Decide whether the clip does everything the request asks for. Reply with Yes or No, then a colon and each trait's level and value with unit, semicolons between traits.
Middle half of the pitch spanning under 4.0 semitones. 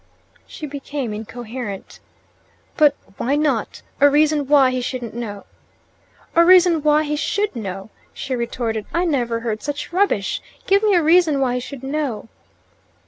No: average, 4.5 semitones